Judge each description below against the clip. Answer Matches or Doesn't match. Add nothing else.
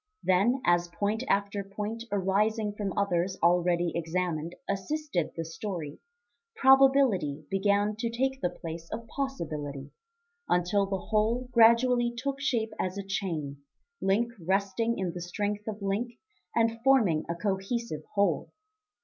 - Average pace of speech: Doesn't match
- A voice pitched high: Matches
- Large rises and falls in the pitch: Doesn't match